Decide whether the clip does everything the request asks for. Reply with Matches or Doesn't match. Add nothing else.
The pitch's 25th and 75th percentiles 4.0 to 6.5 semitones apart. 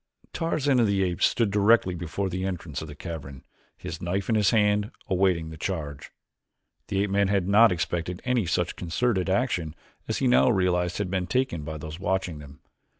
Doesn't match